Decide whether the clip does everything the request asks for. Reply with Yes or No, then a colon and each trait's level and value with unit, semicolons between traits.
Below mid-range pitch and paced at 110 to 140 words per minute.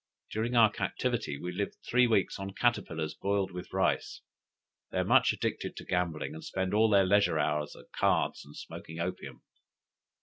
No: very low, 95 Hz; average, 170 wpm